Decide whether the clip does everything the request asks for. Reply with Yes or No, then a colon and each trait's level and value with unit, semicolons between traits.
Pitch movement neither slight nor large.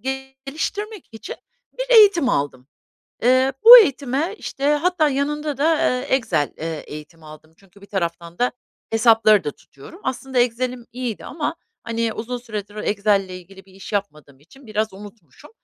No: wide, 6.0 semitones